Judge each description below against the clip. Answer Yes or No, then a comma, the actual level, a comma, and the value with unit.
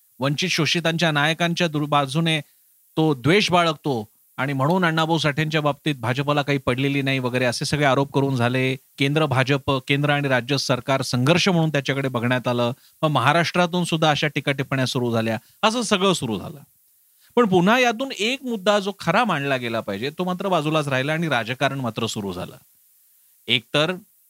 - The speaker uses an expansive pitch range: No, average, 4.3 semitones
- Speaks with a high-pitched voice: No, medium, 145 Hz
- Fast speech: Yes, fast, 160 wpm